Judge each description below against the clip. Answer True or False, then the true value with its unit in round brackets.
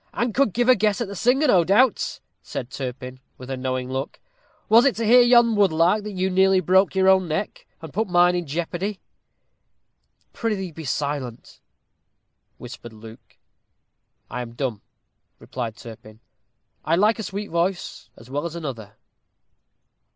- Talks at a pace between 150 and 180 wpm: True (160 wpm)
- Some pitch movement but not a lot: False (8.2 semitones)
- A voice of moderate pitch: True (175 Hz)